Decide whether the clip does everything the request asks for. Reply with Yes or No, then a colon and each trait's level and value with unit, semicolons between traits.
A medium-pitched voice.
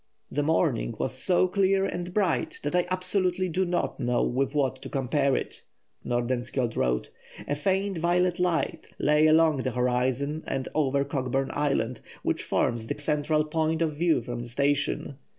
Yes: medium, 150 Hz